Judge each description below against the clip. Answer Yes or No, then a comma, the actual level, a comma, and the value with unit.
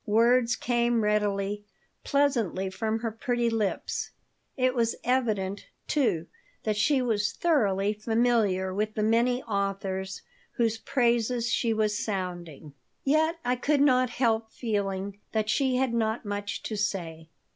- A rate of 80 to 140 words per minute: Yes, slow, 135 wpm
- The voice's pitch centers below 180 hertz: No, high, 220 Hz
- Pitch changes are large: No, average, 3.3 semitones